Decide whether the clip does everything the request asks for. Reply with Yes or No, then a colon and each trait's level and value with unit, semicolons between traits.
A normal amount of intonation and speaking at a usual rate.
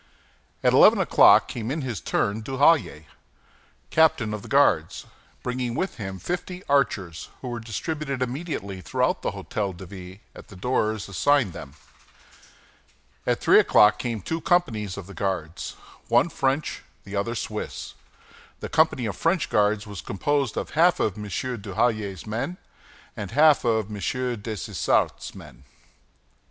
No: wide, 5.7 semitones; average, 145 wpm